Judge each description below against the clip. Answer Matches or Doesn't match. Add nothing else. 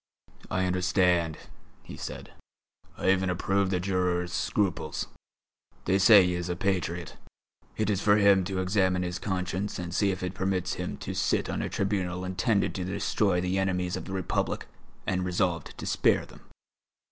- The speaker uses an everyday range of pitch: Doesn't match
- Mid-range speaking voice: Doesn't match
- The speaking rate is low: Doesn't match